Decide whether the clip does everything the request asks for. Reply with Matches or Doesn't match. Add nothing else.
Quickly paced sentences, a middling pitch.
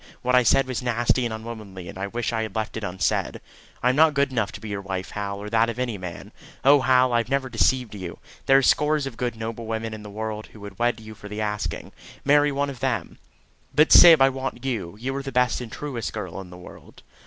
Doesn't match